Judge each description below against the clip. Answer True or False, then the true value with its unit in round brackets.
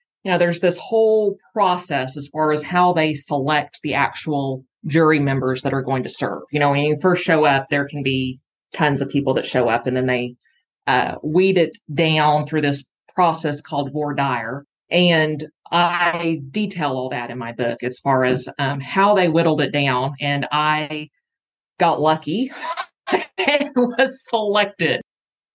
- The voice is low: False (150 Hz)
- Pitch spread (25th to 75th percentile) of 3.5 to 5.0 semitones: True (4.0 semitones)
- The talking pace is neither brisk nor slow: True (175 wpm)